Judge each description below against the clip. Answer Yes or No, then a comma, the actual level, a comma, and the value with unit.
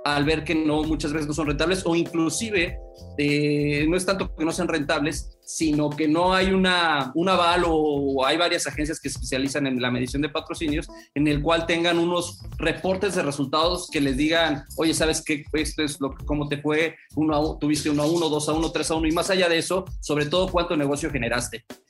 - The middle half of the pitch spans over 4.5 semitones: No, narrow, 2.4 semitones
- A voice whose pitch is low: No, medium, 155 Hz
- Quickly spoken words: Yes, fast, 215 wpm